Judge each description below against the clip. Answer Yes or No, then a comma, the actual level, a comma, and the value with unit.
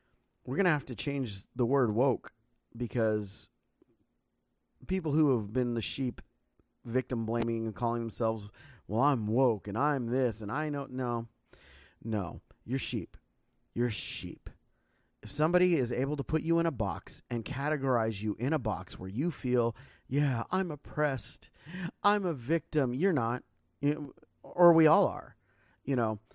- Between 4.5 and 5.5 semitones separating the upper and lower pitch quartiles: Yes, average, 4.8 semitones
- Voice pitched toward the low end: Yes, low, 125 Hz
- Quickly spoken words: No, average, 155 wpm